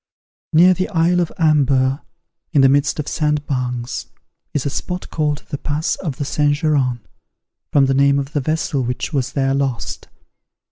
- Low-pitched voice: No, medium, 145 Hz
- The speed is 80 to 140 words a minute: No, average, 170 wpm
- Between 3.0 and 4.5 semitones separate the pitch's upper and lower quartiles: No, narrow, 2.4 semitones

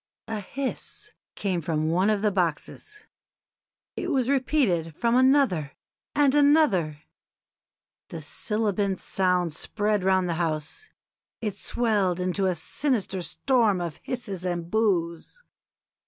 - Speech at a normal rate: No, slow, 120 wpm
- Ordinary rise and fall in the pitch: No, wide, 6.0 semitones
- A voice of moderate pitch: No, high, 195 Hz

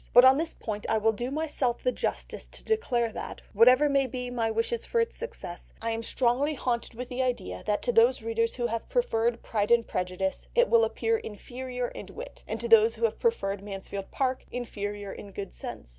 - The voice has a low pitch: No, high, 235 Hz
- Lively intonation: No, average, 3.0 semitones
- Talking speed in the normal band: No, fast, 210 wpm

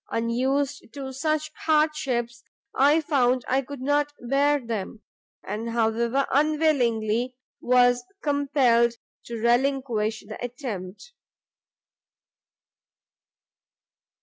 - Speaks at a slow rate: Yes, slow, 85 wpm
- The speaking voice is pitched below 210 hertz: No, very high, 255 Hz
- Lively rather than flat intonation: No, average, 3.5 semitones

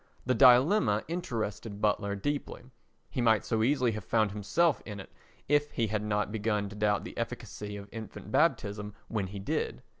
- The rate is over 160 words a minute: Yes, average, 175 wpm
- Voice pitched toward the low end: Yes, low, 110 Hz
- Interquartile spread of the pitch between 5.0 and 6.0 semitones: No, average, 3.0 semitones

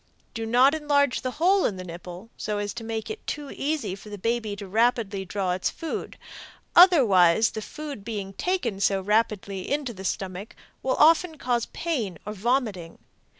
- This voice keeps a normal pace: Yes, average, 170 wpm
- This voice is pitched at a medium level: No, high, 225 Hz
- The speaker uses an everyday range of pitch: No, wide, 6.2 semitones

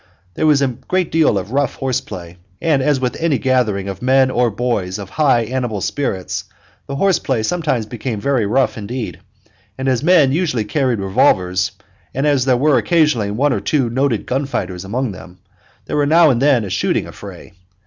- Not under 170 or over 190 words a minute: No, average, 200 wpm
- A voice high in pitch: No, low, 130 Hz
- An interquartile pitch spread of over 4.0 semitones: Yes, average, 5.2 semitones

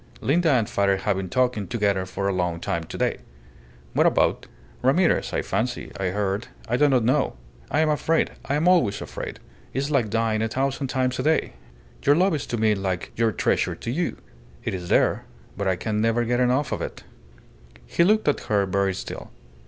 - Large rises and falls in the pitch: Yes, wide, 5.9 semitones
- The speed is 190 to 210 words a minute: Yes, average, 200 wpm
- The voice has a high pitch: No, low, 115 Hz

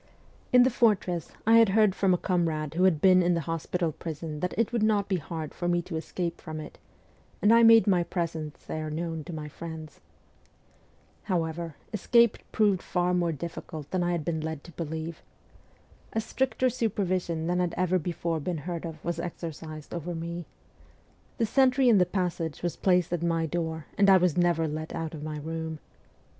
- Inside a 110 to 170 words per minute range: No, average, 190 wpm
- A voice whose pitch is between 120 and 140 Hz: No, medium, 170 Hz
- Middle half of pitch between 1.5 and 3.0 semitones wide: Yes, narrow, 2.6 semitones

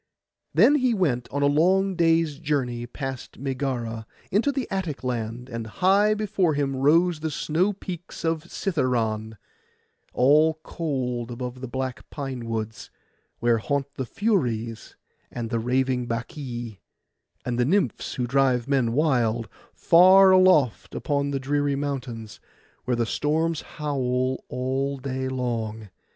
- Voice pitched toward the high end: No, low, 135 Hz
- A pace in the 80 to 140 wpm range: Yes, slow, 135 wpm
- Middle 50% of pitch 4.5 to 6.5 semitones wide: Yes, average, 4.8 semitones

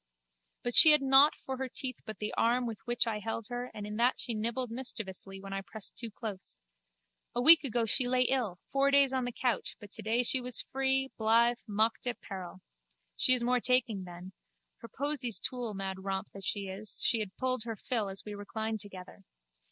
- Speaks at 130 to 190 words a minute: No, fast, 205 wpm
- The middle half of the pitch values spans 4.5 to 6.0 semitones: No, average, 3.7 semitones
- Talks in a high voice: Yes, high, 230 Hz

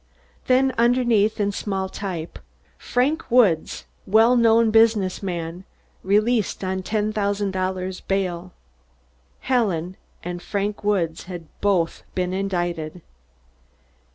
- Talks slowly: Yes, slow, 100 wpm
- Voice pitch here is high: Yes, high, 195 Hz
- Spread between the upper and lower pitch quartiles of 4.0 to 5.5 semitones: No, average, 3.5 semitones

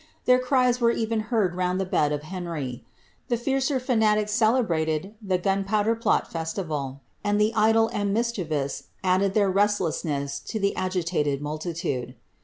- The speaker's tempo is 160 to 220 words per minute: No, average, 145 wpm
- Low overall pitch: No, high, 195 Hz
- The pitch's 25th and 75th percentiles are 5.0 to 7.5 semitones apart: Yes, wide, 5.5 semitones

